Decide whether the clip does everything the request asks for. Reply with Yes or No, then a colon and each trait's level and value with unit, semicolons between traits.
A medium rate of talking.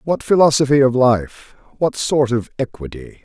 Yes: average, 150 wpm